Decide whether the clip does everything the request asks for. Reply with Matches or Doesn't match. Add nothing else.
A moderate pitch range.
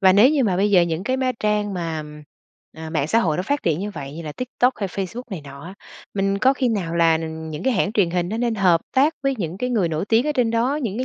Doesn't match